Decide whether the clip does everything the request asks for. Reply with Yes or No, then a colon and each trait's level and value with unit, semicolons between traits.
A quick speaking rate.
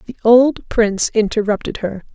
No: average, 140 wpm